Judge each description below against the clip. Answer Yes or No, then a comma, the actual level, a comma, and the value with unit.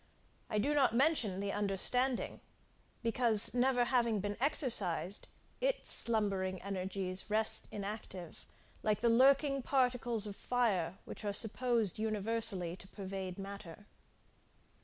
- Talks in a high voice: Yes, high, 215 Hz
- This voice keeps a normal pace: No, slow, 115 wpm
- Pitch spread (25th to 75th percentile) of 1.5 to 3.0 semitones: No, average, 4.0 semitones